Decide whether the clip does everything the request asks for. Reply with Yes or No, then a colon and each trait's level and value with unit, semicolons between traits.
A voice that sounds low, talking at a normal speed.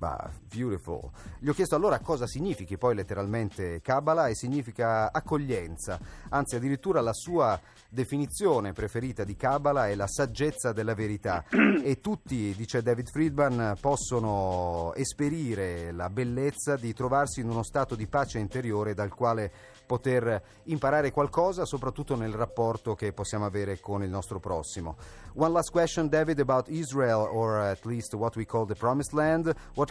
Yes: low, 120 Hz; average, 150 wpm